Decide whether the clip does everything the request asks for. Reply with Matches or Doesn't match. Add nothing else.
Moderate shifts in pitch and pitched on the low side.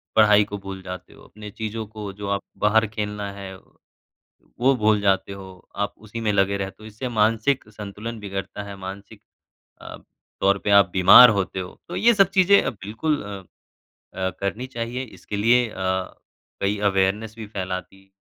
Doesn't match